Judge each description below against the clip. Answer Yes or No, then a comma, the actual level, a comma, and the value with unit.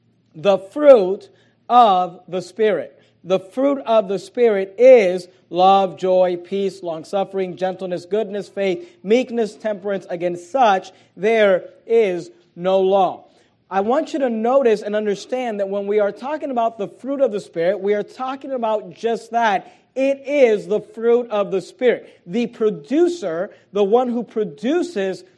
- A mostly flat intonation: No, average, 3.9 semitones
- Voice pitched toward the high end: Yes, high, 205 Hz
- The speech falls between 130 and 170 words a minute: Yes, average, 150 wpm